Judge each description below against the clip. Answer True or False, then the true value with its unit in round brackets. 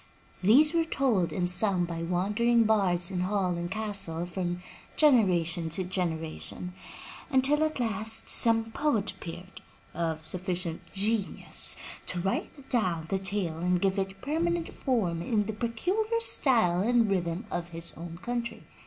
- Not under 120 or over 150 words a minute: True (145 wpm)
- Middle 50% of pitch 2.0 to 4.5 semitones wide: False (5.0 semitones)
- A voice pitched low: False (195 Hz)